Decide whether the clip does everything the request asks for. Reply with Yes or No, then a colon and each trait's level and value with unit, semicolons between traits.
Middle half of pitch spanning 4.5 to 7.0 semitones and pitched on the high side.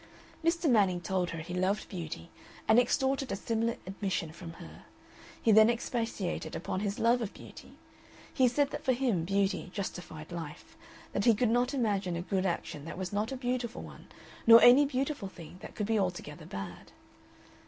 Yes: average, 5.3 semitones; high, 205 Hz